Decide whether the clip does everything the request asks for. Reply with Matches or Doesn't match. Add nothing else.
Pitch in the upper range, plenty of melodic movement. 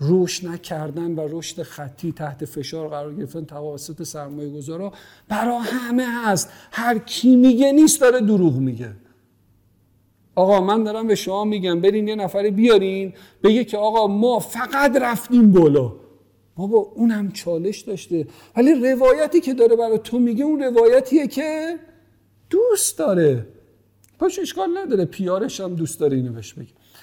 Matches